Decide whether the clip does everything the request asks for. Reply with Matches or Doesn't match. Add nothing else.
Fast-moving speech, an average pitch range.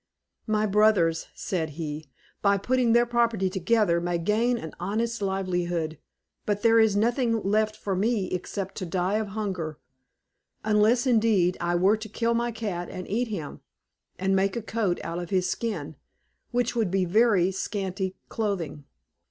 Doesn't match